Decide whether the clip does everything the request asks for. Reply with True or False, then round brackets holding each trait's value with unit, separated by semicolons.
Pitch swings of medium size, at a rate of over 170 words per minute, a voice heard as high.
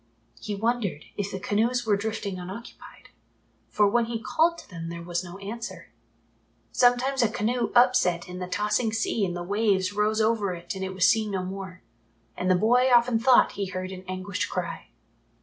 True (3.9 semitones; 185 wpm; 205 Hz)